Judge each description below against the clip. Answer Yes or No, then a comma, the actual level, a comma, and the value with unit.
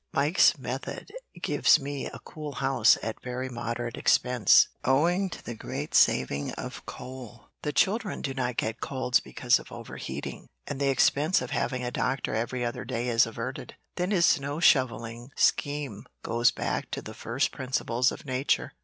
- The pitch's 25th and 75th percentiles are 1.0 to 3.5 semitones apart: Yes, average, 3.2 semitones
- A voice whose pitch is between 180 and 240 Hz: No, low, 130 Hz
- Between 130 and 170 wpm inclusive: Yes, average, 165 wpm